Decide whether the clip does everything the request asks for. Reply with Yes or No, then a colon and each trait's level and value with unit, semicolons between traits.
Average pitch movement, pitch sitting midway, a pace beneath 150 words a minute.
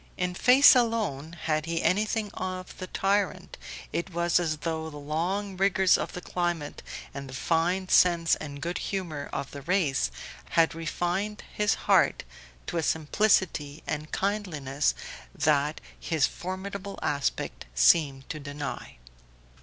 Yes: average, 4.2 semitones; medium, 170 Hz; average, 140 wpm